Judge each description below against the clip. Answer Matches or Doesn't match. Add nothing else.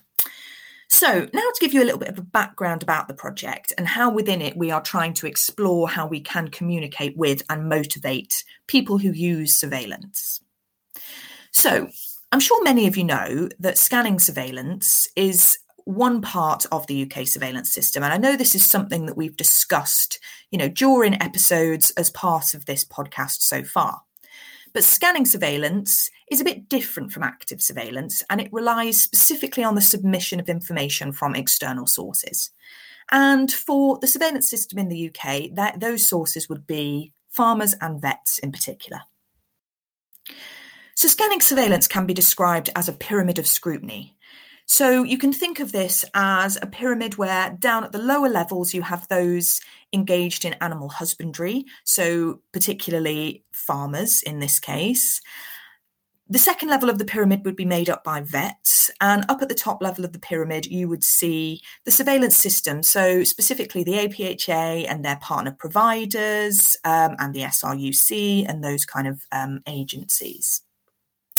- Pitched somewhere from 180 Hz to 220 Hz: Matches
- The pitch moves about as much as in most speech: Doesn't match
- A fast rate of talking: Doesn't match